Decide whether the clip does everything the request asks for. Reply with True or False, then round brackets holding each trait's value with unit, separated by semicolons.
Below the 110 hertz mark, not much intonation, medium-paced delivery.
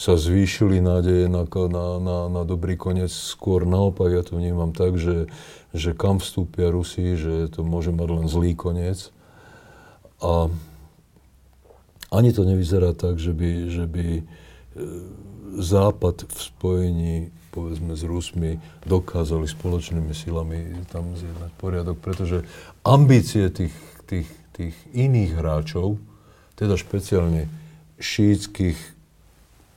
True (90 Hz; 2.0 semitones; 120 wpm)